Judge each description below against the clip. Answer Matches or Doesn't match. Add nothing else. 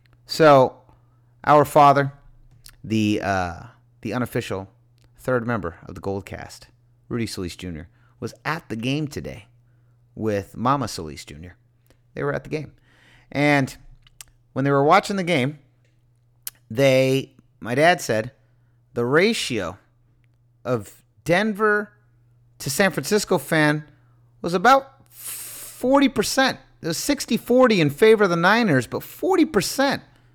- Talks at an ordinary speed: Doesn't match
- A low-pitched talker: Matches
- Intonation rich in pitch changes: Doesn't match